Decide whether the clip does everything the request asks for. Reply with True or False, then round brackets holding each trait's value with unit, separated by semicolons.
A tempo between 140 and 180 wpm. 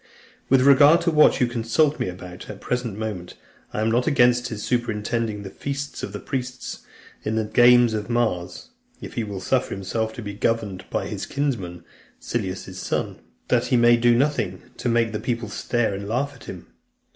False (190 wpm)